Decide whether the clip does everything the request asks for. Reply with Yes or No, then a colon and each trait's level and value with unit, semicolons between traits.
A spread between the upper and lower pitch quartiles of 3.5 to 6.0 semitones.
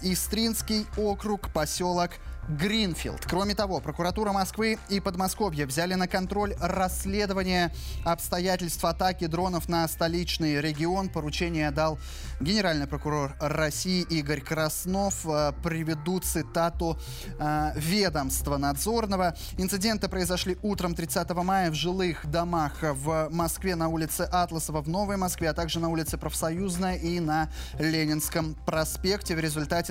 No: average, 3.1 semitones